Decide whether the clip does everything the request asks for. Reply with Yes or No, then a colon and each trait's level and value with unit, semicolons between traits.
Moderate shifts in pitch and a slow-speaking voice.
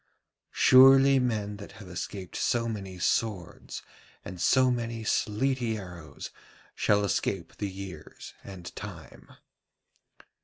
Yes: average, 4.1 semitones; slow, 110 wpm